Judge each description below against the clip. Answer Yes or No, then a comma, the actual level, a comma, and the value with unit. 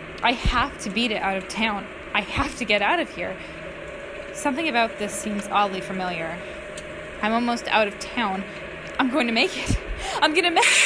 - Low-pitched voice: No, high, 210 Hz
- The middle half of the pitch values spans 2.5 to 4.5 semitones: Yes, average, 3.5 semitones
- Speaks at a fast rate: No, average, 195 wpm